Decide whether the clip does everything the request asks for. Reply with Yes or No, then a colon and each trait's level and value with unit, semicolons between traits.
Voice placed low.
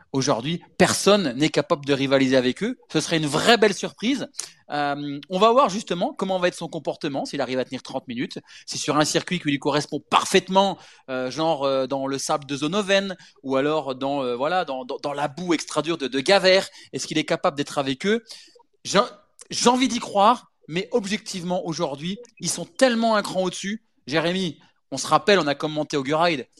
No: medium, 165 Hz